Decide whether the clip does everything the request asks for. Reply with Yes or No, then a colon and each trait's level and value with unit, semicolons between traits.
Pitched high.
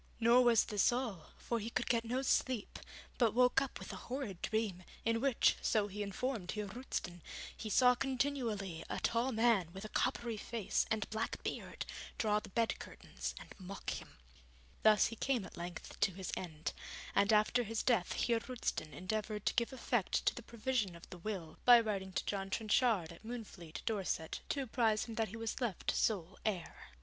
Yes: high, 220 Hz